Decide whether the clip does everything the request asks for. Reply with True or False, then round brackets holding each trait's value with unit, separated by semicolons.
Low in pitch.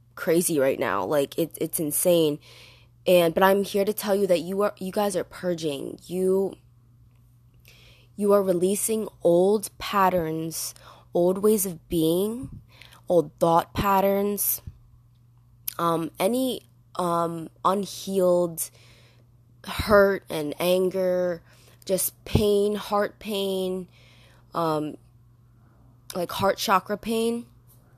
False (170 Hz)